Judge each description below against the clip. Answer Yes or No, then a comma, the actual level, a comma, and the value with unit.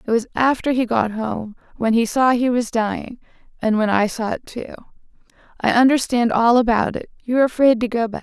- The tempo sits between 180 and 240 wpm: Yes, average, 195 wpm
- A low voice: No, high, 235 Hz